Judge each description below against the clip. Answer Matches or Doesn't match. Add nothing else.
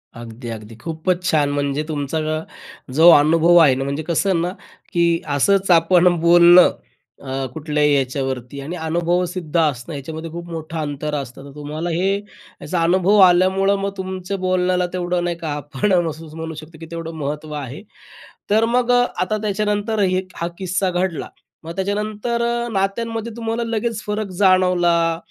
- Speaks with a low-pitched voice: Doesn't match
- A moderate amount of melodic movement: Matches